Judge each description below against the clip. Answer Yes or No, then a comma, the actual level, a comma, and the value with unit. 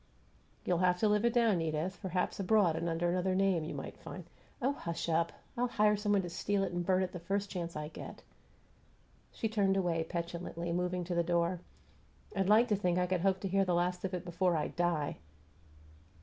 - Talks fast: Yes, fast, 220 wpm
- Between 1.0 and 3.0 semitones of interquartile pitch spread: Yes, narrow, 2.4 semitones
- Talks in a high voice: No, medium, 180 Hz